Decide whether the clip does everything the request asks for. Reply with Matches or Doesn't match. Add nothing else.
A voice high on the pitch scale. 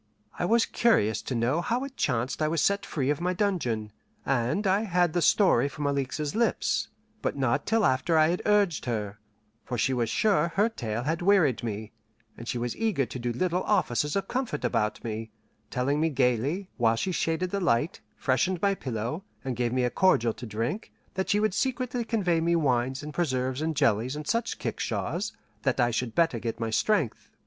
Doesn't match